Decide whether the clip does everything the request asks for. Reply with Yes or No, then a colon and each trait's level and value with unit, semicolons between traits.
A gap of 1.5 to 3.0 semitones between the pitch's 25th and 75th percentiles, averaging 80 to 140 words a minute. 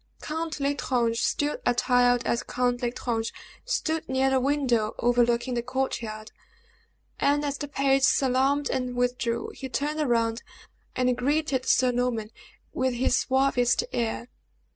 Yes: narrow, 2.4 semitones; slow, 135 wpm